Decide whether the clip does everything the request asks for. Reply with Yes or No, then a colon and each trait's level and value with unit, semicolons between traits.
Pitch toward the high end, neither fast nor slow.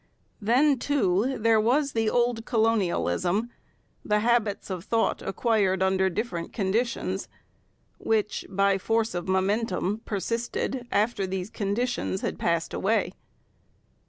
No: high, 215 Hz; slow, 115 wpm